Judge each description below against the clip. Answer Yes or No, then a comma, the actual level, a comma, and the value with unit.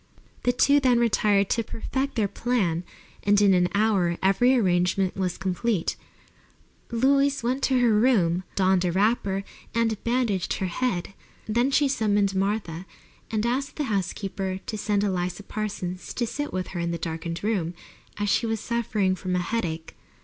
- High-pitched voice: Yes, high, 205 Hz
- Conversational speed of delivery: Yes, average, 165 wpm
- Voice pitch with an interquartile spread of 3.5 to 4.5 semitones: Yes, average, 4.2 semitones